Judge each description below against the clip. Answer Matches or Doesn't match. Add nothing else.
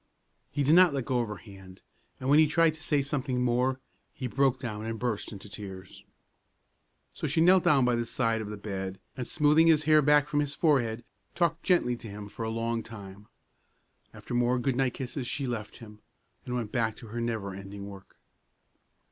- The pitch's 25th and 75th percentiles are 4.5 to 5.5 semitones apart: Matches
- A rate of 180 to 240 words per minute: Matches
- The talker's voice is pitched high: Doesn't match